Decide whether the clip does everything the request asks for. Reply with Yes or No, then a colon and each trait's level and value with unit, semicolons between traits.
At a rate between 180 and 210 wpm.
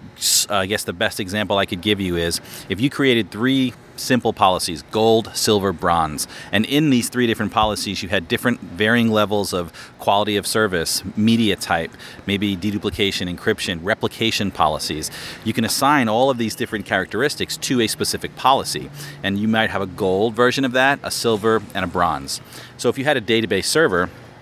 Yes: average, 185 wpm